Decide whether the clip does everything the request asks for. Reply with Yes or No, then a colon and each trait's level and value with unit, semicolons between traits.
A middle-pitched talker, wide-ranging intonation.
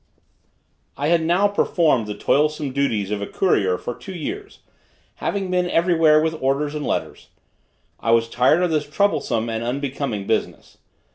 Yes: medium, 150 Hz; wide, 6.6 semitones